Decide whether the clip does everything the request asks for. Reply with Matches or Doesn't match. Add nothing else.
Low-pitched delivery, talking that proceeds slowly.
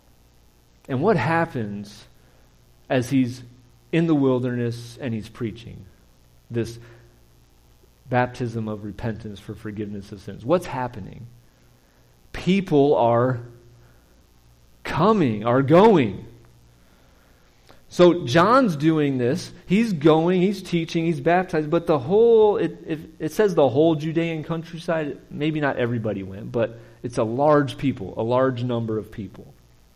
Matches